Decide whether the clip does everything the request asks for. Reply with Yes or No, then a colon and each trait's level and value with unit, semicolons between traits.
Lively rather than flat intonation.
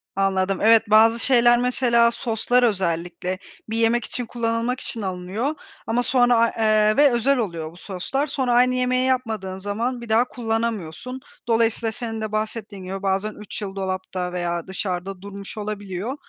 No: average, 3.8 semitones